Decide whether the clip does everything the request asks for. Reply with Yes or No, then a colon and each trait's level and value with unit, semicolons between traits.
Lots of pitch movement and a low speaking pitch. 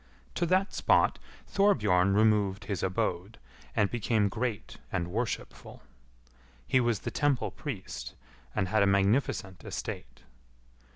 No: average, 4.0 semitones; low, 105 Hz